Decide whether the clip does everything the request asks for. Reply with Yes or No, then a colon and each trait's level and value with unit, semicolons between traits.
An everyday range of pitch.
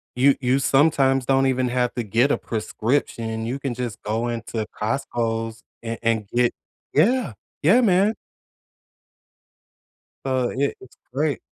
Yes: average, 3.3 semitones